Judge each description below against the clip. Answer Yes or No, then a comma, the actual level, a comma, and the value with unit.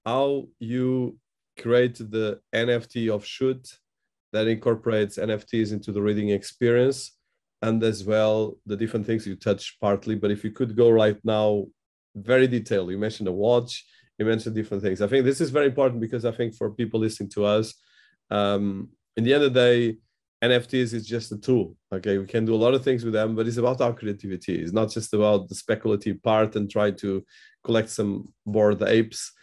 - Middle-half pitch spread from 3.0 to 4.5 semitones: No, narrow, 2.5 semitones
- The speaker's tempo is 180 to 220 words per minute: Yes, average, 195 wpm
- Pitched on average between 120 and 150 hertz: No, low, 110 Hz